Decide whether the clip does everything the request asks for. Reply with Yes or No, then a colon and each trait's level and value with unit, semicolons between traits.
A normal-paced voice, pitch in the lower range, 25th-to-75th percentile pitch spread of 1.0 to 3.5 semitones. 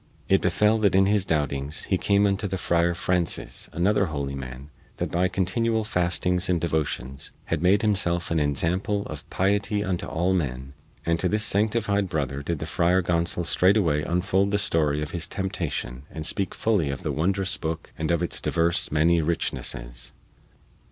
No: average, 170 wpm; very low, 85 Hz; average, 4.0 semitones